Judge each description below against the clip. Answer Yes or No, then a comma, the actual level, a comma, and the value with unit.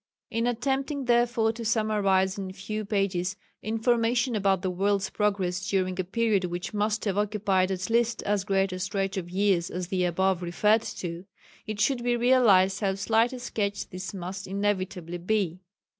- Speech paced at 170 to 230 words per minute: Yes, average, 175 wpm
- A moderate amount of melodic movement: Yes, average, 3.0 semitones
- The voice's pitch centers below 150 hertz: No, high, 200 Hz